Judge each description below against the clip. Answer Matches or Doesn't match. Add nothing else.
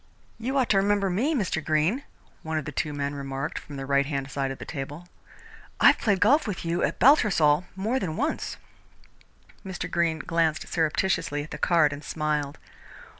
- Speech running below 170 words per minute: Doesn't match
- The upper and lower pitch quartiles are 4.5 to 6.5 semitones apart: Matches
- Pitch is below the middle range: Doesn't match